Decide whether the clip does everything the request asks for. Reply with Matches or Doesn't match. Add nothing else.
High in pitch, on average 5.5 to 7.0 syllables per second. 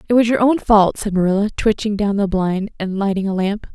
Matches